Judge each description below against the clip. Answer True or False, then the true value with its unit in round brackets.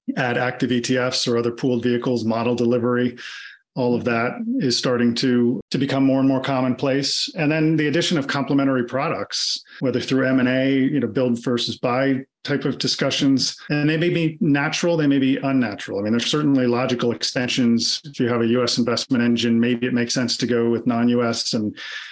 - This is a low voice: True (125 Hz)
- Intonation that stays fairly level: True (2.2 semitones)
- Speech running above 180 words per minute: True (195 wpm)